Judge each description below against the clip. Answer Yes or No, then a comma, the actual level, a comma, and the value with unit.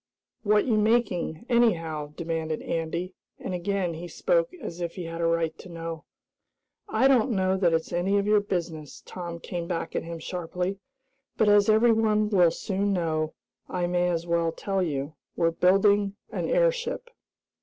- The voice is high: No, medium, 180 Hz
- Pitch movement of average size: Yes, average, 3.8 semitones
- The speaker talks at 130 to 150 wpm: No, average, 165 wpm